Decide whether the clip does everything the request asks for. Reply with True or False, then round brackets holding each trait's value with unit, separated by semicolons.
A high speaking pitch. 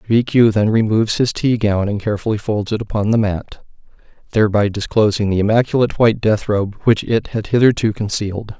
False (110 Hz)